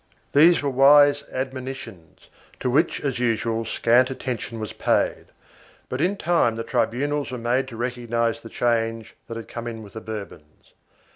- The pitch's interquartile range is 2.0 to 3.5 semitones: Yes, average, 3.0 semitones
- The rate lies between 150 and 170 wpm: Yes, average, 165 wpm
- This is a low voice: Yes, low, 120 Hz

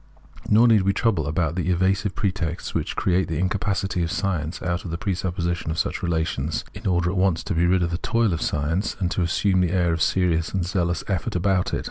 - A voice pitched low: Yes, very low, 90 Hz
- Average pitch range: No, narrow, 2.3 semitones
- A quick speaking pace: Yes, fast, 230 wpm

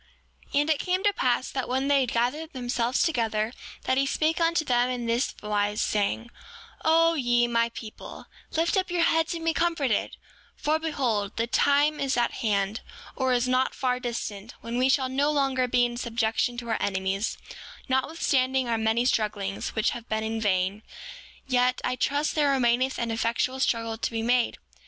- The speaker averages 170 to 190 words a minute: Yes, average, 185 wpm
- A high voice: Yes, very high, 250 Hz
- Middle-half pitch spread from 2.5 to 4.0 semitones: Yes, average, 3.5 semitones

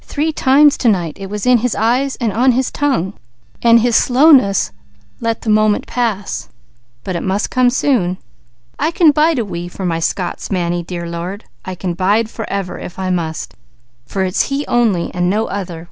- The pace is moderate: Yes, average, 160 wpm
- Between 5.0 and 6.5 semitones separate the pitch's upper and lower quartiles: Yes, average, 5.3 semitones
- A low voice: No, high, 210 Hz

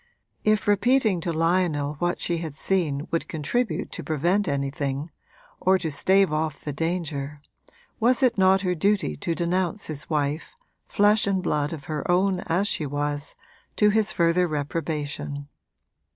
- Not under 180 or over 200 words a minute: No, average, 150 wpm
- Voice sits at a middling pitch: Yes, medium, 170 Hz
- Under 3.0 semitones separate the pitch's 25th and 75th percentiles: No, average, 4.5 semitones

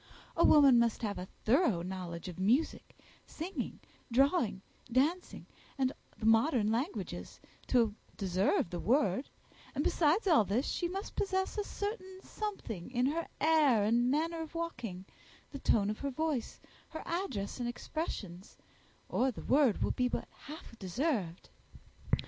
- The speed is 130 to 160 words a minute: Yes, average, 145 wpm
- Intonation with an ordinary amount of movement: No, wide, 7.5 semitones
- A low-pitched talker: No, very high, 255 Hz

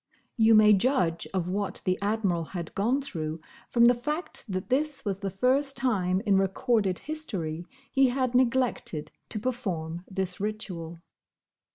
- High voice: Yes, high, 205 Hz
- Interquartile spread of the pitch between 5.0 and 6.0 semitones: Yes, wide, 5.6 semitones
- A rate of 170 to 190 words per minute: No, average, 150 wpm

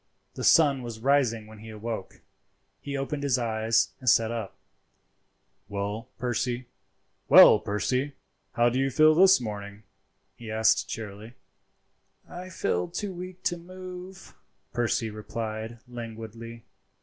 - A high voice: No, low, 115 Hz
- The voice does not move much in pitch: No, average, 4.3 semitones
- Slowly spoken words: Yes, slow, 120 wpm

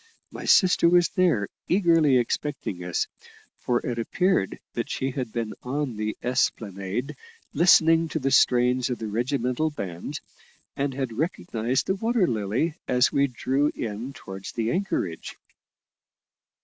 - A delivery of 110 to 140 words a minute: Yes, slow, 135 wpm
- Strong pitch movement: Yes, wide, 5.7 semitones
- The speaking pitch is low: Yes, low, 125 Hz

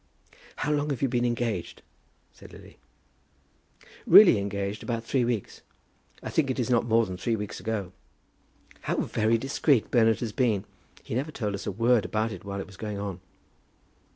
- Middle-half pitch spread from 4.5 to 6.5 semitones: No, average, 3.3 semitones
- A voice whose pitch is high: No, low, 115 Hz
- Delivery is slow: No, average, 180 wpm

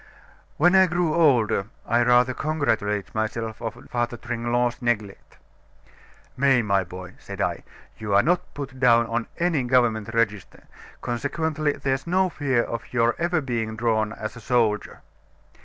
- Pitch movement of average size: Yes, average, 4.1 semitones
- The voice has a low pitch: Yes, low, 120 Hz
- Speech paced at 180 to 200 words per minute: No, average, 145 wpm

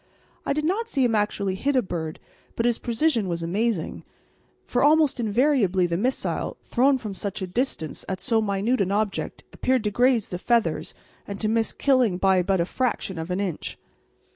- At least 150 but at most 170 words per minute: No, average, 190 wpm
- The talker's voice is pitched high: Yes, high, 215 Hz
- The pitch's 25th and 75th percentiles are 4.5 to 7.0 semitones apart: Yes, average, 5.1 semitones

